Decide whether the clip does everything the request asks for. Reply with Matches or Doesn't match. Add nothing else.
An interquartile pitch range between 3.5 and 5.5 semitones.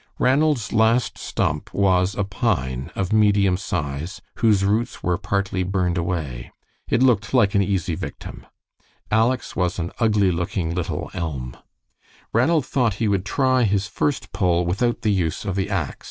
Matches